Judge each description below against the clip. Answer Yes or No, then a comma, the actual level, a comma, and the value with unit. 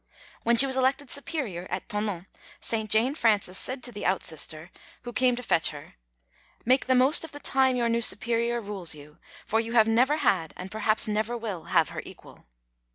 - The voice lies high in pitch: Yes, high, 225 Hz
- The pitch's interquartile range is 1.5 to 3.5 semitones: No, average, 4.8 semitones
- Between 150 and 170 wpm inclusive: No, average, 195 wpm